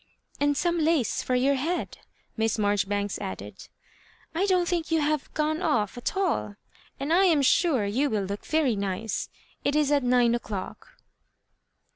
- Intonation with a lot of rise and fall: Yes, wide, 7.1 semitones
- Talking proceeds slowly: No, average, 165 wpm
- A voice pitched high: Yes, very high, 275 Hz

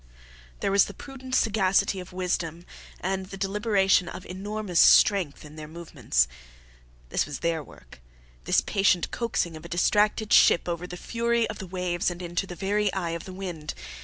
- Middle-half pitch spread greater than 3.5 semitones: No, average, 2.8 semitones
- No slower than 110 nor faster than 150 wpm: No, average, 175 wpm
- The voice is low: No, medium, 185 Hz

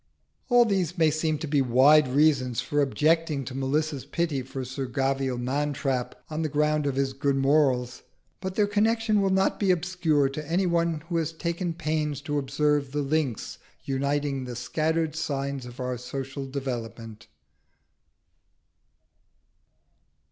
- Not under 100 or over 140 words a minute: No, average, 150 wpm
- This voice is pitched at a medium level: Yes, medium, 145 Hz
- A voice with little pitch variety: No, average, 3.3 semitones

